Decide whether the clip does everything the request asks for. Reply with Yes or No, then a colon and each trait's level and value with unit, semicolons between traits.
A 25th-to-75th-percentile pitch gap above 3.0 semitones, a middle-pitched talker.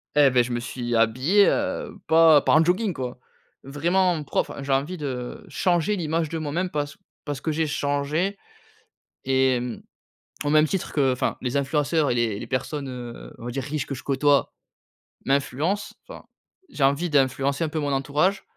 Yes: average, 3.5 semitones; medium, 145 Hz